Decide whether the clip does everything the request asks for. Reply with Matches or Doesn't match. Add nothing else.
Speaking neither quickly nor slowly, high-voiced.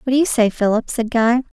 Doesn't match